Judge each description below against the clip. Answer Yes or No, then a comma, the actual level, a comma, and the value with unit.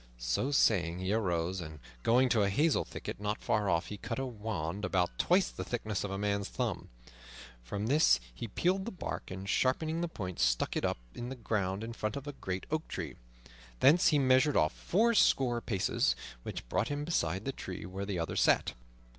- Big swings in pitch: Yes, wide, 6.3 semitones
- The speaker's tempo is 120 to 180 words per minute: No, average, 200 wpm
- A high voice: No, low, 105 Hz